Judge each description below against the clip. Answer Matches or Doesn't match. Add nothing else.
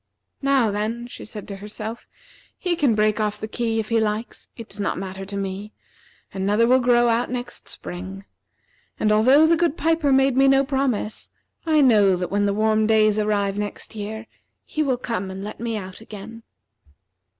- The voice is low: Doesn't match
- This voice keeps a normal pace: Matches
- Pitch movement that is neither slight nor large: Matches